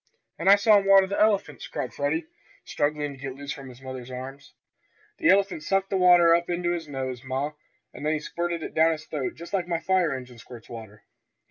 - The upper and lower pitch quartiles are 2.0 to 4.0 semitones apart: No, average, 5.0 semitones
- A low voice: No, medium, 155 Hz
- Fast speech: Yes, fast, 220 wpm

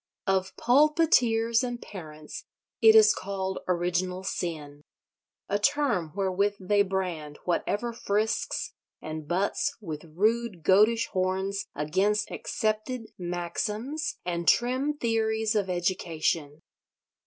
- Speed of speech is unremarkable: No, slow, 105 wpm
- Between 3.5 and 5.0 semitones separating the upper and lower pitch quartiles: Yes, average, 4.5 semitones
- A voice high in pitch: Yes, high, 195 Hz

